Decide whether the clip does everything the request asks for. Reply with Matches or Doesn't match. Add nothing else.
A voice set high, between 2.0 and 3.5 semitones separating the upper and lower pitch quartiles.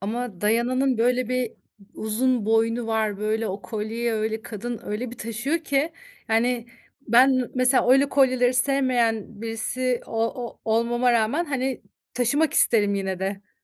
Matches